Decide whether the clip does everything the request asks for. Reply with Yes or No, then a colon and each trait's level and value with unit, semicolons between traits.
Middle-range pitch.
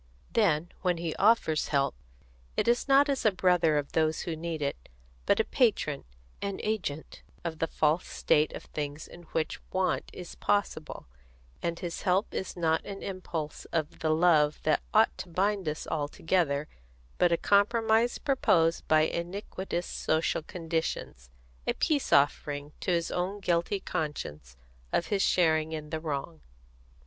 Yes: medium, 170 Hz